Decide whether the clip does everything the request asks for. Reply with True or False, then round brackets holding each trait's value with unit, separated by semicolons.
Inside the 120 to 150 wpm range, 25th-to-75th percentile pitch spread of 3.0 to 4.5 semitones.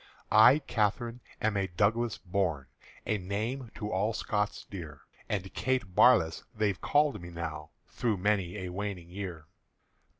True (140 wpm; 3.6 semitones)